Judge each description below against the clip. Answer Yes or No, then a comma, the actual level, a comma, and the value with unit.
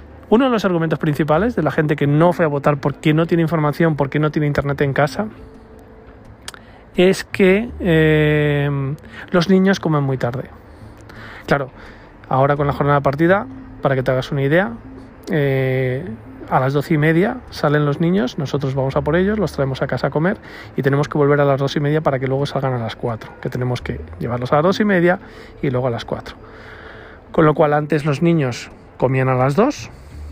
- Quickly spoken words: Yes, fast, 205 wpm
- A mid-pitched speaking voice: Yes, medium, 145 Hz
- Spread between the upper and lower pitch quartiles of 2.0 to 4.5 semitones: Yes, average, 3.9 semitones